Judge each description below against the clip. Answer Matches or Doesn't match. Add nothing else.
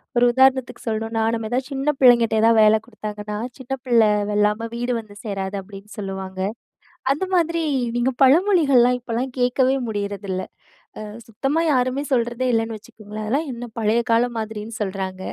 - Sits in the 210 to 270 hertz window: Matches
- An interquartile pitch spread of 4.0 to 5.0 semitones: Doesn't match